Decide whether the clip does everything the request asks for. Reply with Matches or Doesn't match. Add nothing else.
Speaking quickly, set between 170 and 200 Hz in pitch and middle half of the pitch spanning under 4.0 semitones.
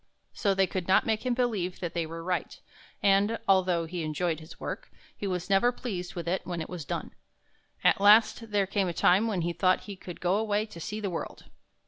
Matches